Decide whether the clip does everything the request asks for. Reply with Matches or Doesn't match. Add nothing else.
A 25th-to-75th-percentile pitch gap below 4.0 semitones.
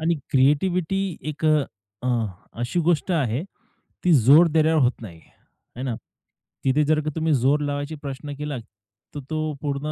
Matches